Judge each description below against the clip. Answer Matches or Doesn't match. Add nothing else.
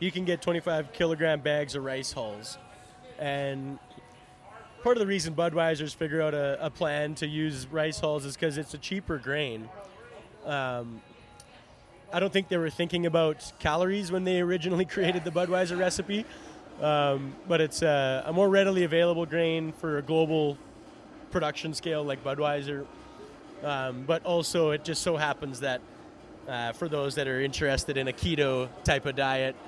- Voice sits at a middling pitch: Matches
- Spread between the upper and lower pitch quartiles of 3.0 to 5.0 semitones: Matches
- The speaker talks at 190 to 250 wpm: Doesn't match